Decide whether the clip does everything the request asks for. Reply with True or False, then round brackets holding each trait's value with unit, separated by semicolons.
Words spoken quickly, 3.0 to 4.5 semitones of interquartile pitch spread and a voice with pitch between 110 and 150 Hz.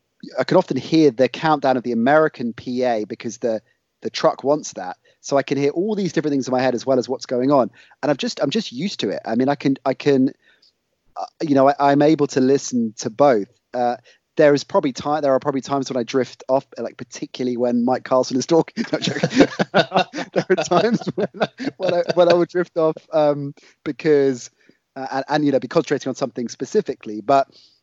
True (220 wpm; 4.2 semitones; 140 Hz)